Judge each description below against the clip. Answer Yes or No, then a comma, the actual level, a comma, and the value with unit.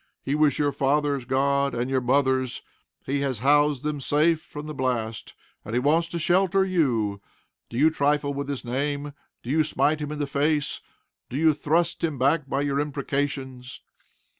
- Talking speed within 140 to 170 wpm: No, average, 180 wpm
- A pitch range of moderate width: No, narrow, 2.2 semitones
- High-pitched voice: No, medium, 140 Hz